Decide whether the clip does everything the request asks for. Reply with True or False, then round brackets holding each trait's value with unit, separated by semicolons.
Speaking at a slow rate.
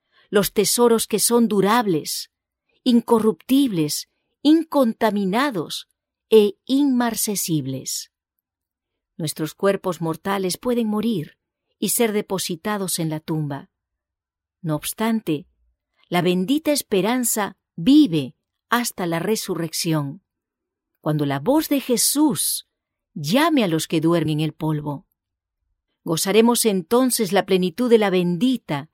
True (100 wpm)